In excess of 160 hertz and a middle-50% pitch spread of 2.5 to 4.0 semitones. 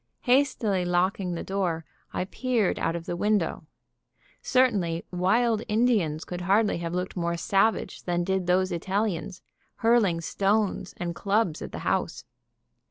Yes: high, 190 Hz; average, 3.7 semitones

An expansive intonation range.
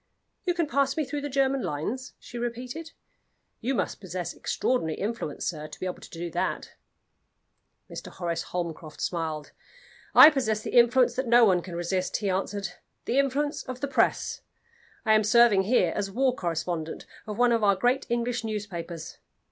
Yes: wide, 6.3 semitones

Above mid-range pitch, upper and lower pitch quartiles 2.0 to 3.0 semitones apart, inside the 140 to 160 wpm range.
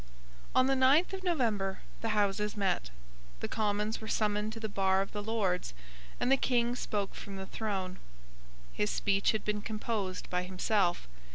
No: high, 210 Hz; average, 2.7 semitones; average, 170 wpm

